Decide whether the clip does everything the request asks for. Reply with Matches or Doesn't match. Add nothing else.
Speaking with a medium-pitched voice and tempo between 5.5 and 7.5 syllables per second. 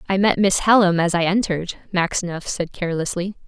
Matches